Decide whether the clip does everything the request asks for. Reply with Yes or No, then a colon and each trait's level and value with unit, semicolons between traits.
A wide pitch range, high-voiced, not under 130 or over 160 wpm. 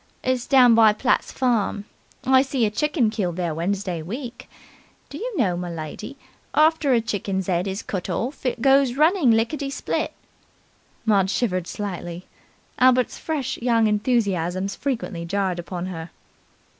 Yes: wide, 5.8 semitones; high, 220 Hz; average, 145 wpm